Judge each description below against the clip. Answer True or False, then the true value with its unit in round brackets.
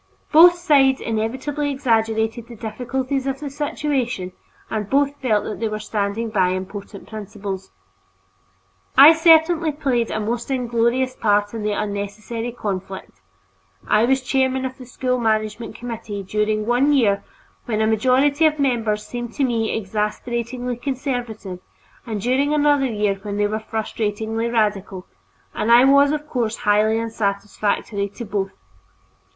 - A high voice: True (230 Hz)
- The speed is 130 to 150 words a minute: True (145 wpm)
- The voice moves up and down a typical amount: True (3.8 semitones)